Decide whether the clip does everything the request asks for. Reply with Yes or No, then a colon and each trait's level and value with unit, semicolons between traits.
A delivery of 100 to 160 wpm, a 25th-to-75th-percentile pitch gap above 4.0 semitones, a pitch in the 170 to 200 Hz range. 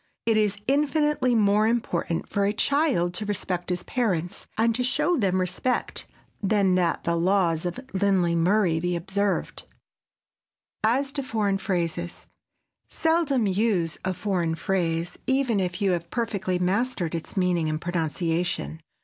Yes: average, 145 wpm; average, 4.4 semitones; high, 190 Hz